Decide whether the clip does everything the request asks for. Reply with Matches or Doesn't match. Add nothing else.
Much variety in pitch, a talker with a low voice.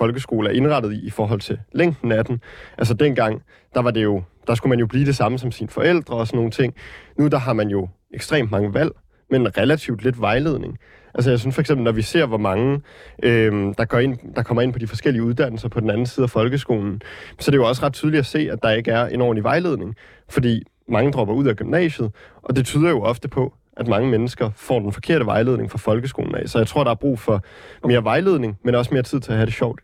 Doesn't match